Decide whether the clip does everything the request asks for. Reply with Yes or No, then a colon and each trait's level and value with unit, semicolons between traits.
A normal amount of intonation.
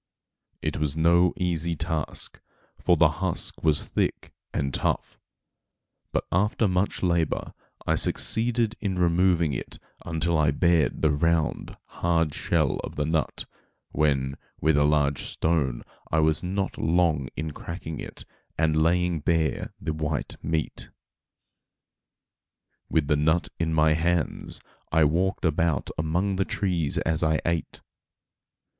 No: narrow, 2.2 semitones